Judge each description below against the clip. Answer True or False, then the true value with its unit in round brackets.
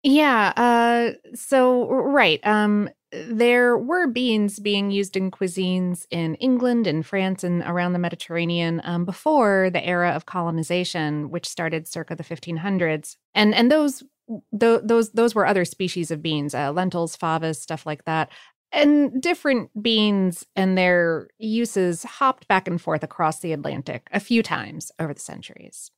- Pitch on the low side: False (190 Hz)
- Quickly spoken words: False (155 wpm)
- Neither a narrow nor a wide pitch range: False (5.7 semitones)